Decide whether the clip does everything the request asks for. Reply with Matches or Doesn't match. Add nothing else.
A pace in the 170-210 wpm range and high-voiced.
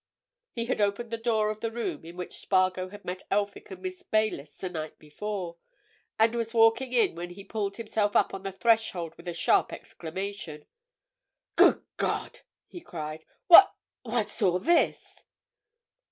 Doesn't match